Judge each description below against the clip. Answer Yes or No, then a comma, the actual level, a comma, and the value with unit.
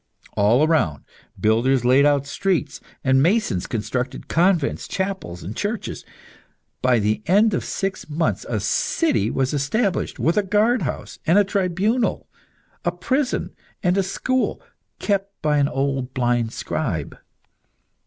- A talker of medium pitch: Yes, medium, 160 Hz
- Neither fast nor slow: No, slow, 130 wpm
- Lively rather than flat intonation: Yes, wide, 7.3 semitones